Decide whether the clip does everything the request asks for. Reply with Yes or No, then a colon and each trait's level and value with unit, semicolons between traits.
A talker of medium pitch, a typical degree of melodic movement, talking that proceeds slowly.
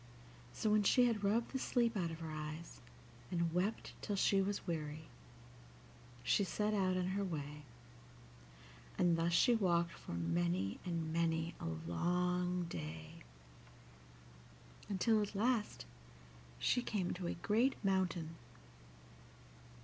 Yes: medium, 180 Hz; average, 4.2 semitones; slow, 130 wpm